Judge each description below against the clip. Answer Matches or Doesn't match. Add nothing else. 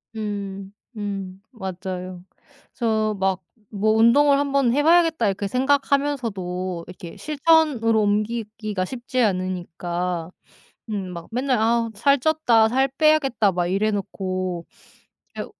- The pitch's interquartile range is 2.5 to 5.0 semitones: Doesn't match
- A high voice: Matches